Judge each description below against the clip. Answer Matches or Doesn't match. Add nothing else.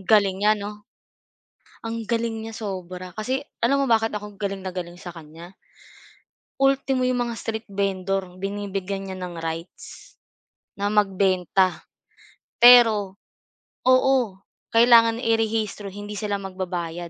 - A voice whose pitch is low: Doesn't match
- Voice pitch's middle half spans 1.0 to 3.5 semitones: Matches